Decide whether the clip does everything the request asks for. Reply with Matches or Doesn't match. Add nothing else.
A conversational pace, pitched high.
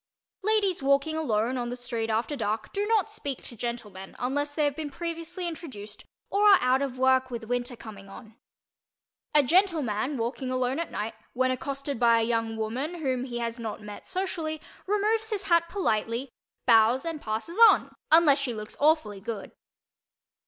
Matches